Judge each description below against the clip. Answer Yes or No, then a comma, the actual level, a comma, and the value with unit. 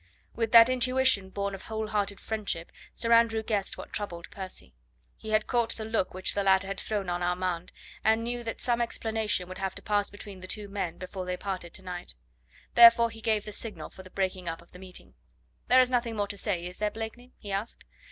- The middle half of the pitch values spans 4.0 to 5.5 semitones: No, average, 3.3 semitones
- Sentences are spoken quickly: Yes, fast, 220 wpm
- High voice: Yes, high, 205 Hz